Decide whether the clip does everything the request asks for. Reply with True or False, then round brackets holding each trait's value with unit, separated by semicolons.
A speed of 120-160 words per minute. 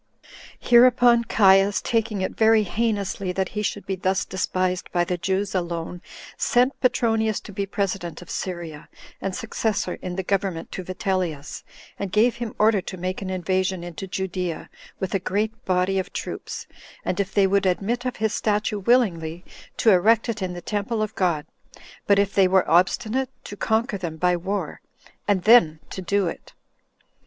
False (175 wpm)